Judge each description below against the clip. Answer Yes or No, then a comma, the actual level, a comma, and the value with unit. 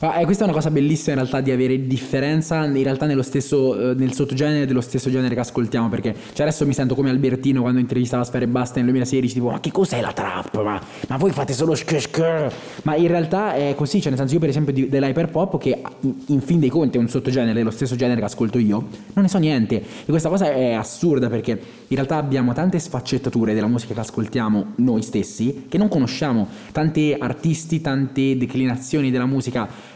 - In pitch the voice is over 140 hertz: No, low, 135 Hz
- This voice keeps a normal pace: No, fast, 205 wpm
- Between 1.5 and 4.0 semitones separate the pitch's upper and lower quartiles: Yes, average, 3.7 semitones